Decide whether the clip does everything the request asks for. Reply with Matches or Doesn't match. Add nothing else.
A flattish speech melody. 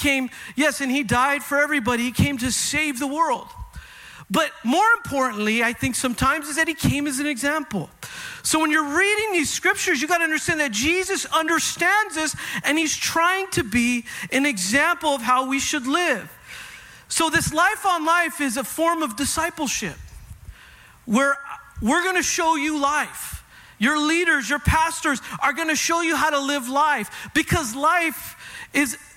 Doesn't match